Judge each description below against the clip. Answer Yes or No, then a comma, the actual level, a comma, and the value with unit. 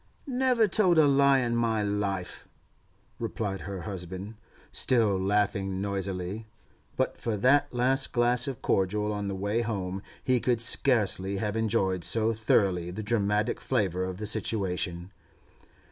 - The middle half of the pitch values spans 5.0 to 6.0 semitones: No, average, 3.7 semitones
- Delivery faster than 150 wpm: No, average, 140 wpm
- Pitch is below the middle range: Yes, low, 105 Hz